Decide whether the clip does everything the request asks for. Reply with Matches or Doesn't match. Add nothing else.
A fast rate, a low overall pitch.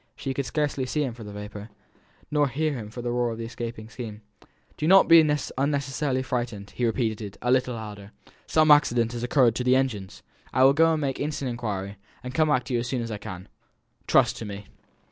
Matches